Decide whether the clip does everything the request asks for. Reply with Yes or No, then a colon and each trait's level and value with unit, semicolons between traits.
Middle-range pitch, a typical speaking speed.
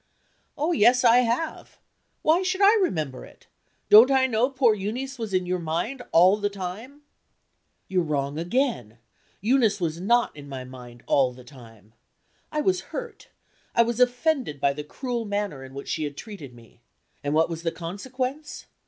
No: high, 205 Hz; average, 170 wpm